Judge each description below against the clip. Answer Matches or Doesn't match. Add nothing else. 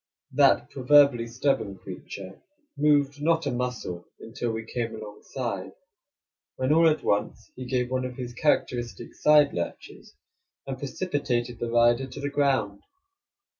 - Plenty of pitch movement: Doesn't match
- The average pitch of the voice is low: Matches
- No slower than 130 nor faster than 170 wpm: Matches